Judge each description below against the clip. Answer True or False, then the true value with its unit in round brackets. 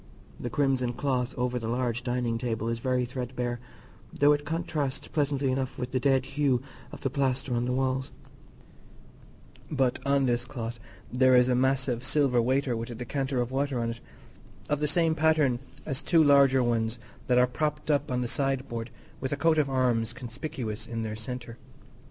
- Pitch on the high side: False (130 Hz)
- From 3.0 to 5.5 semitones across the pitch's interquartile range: False (2.4 semitones)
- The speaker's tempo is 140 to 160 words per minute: False (180 wpm)